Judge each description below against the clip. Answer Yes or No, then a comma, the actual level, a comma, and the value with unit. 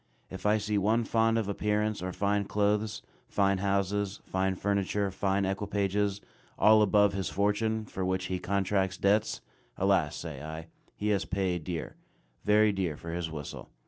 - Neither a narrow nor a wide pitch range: No, narrow, 1.7 semitones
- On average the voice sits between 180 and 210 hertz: No, low, 100 Hz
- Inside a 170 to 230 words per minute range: No, average, 160 wpm